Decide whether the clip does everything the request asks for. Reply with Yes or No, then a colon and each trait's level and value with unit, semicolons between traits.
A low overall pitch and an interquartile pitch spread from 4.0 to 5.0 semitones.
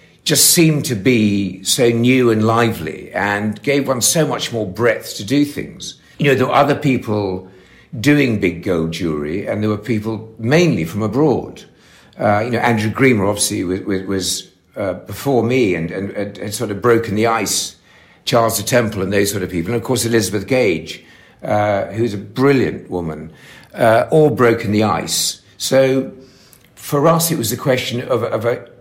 Yes: low, 115 Hz; average, 4.3 semitones